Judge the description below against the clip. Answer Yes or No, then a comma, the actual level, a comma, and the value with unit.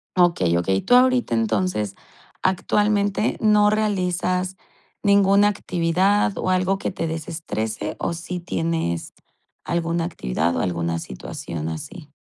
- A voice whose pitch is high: No, medium, 175 Hz